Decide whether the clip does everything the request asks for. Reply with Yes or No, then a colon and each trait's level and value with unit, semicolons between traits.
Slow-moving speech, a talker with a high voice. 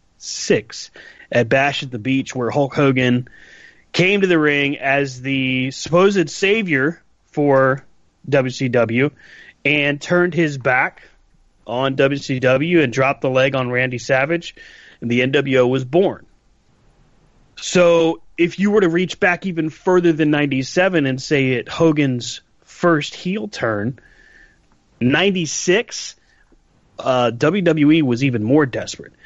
No: slow, 125 wpm; medium, 140 Hz